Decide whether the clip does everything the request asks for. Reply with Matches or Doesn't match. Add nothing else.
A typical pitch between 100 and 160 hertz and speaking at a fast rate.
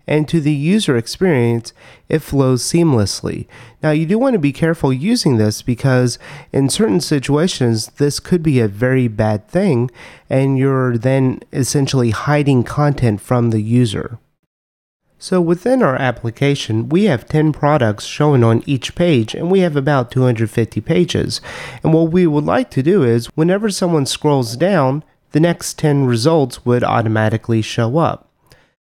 Doesn't match